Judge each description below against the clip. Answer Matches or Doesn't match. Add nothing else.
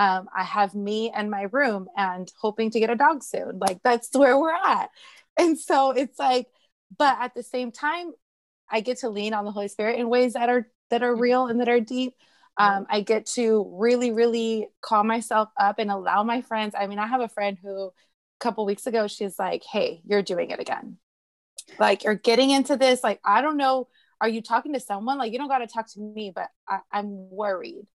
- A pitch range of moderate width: Matches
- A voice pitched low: Doesn't match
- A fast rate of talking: Matches